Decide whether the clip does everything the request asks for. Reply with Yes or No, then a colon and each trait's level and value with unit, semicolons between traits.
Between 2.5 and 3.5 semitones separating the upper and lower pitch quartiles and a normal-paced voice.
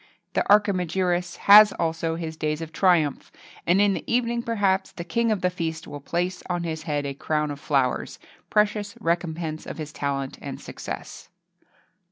No: average, 3.9 semitones; average, 170 wpm